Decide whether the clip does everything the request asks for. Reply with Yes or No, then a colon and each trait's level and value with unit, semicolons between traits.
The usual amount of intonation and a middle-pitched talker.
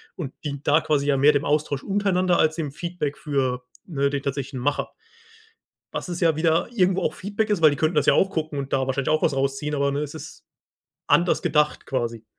Yes: average, 3.4 semitones; medium, 150 Hz